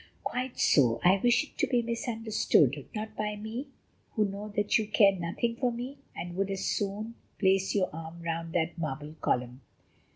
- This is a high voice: Yes, high, 200 Hz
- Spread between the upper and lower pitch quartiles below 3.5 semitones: No, average, 5.2 semitones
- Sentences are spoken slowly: No, average, 175 wpm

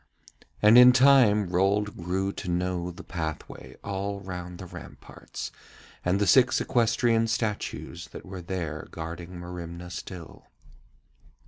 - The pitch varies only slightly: No, average, 3.2 semitones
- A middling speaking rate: No, slow, 125 wpm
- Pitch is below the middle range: Yes, very low, 95 Hz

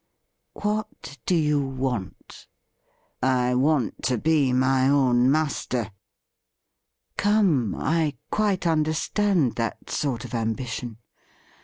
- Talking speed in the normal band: No, slow, 120 wpm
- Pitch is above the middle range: No, low, 135 Hz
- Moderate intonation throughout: Yes, average, 4.2 semitones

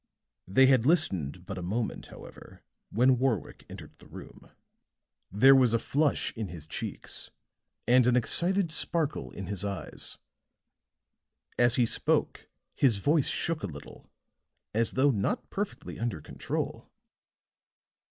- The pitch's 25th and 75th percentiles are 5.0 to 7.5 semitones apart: Yes, wide, 5.6 semitones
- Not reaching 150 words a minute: Yes, slow, 135 wpm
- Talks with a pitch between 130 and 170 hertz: No, low, 120 Hz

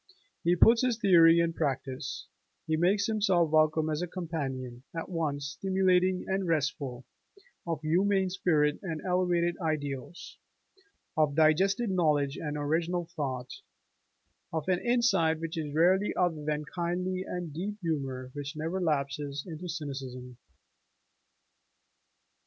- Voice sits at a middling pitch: Yes, medium, 165 Hz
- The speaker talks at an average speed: No, slow, 130 wpm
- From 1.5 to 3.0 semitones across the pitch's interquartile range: No, average, 3.6 semitones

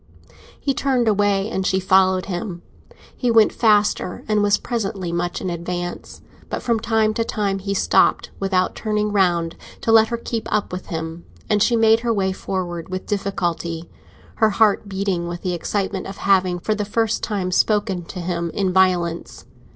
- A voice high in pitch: Yes, high, 195 Hz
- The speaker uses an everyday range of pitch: Yes, average, 3.0 semitones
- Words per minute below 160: No, average, 175 wpm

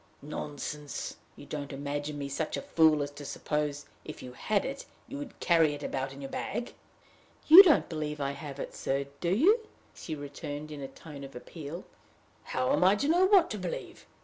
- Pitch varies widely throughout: No, average, 4.3 semitones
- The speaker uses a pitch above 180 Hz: No, medium, 150 Hz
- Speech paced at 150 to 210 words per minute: Yes, average, 200 wpm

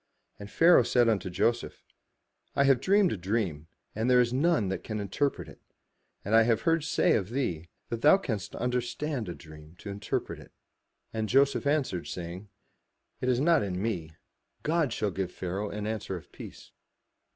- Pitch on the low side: Yes, low, 110 Hz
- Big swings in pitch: Yes, wide, 5.9 semitones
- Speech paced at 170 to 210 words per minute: Yes, average, 180 wpm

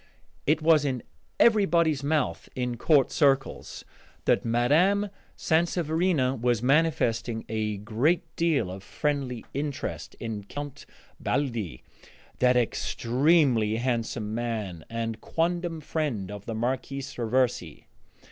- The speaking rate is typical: No, slow, 110 wpm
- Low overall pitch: Yes, low, 130 Hz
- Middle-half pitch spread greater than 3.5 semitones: Yes, wide, 5.4 semitones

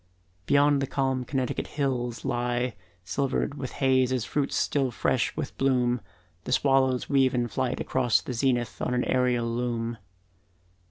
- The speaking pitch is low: Yes, low, 125 Hz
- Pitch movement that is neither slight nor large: No, narrow, 1.8 semitones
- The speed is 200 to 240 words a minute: No, average, 155 wpm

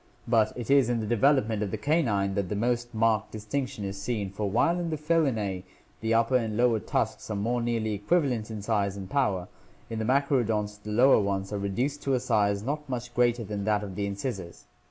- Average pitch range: Yes, average, 3.5 semitones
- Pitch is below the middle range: Yes, low, 110 Hz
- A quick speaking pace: Yes, fast, 215 wpm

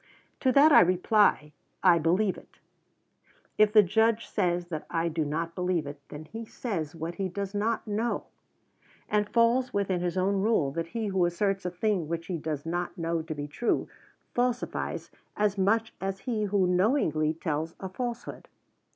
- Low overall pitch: No, medium, 185 Hz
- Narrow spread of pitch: No, average, 4.3 semitones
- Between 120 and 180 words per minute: Yes, average, 175 wpm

